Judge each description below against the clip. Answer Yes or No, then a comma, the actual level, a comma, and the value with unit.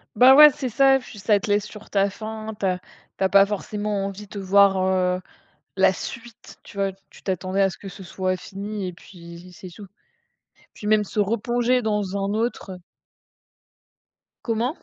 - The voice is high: Yes, high, 200 Hz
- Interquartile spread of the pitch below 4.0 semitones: Yes, narrow, 2.4 semitones